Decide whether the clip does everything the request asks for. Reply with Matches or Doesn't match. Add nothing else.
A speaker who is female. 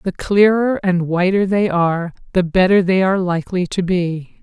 Matches